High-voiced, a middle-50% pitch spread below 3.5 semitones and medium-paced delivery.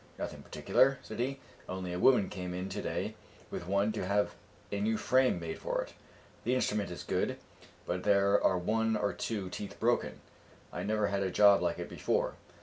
No: low, 100 Hz; average, 3.0 semitones; average, 195 wpm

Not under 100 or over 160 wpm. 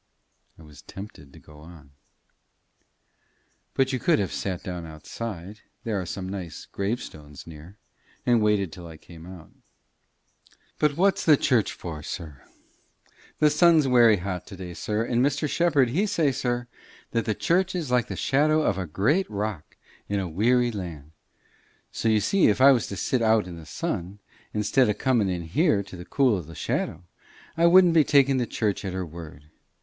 No: average, 185 wpm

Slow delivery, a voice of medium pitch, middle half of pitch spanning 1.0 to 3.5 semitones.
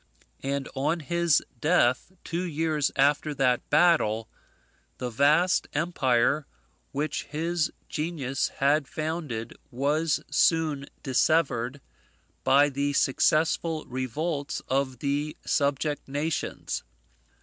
Yes: slow, 95 wpm; medium, 145 Hz; average, 2.9 semitones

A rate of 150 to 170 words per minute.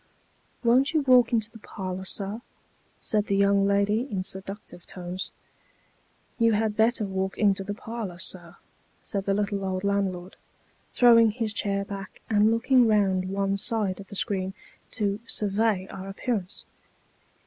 Yes: average, 155 wpm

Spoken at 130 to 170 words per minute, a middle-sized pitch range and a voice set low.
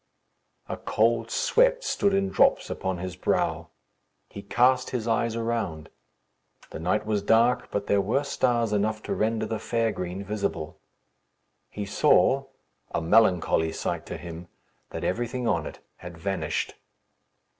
Yes: average, 145 wpm; average, 4.3 semitones; low, 110 Hz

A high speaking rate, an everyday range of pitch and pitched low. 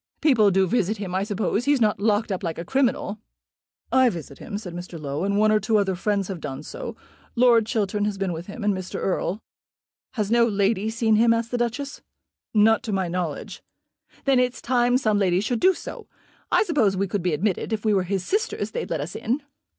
No: fast, 220 wpm; average, 3.7 semitones; high, 210 Hz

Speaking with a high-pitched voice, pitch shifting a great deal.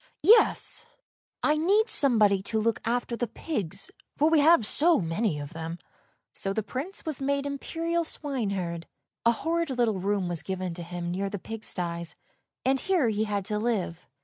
Yes: high, 220 Hz; wide, 7.4 semitones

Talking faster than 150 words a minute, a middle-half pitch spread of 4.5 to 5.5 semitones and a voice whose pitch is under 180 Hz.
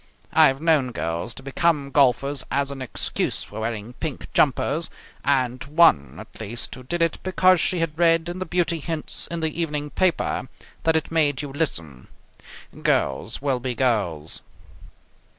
Yes: average, 165 wpm; average, 4.9 semitones; medium, 140 Hz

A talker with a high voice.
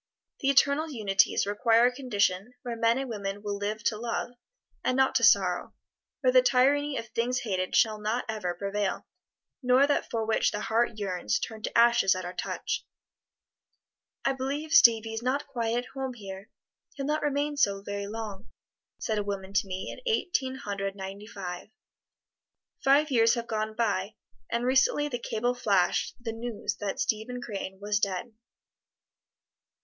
Yes: high, 225 Hz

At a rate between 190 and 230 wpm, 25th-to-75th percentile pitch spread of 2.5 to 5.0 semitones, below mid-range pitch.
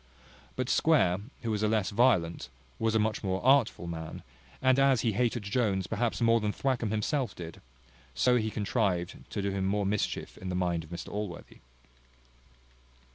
No: average, 175 wpm; average, 4.2 semitones; low, 105 Hz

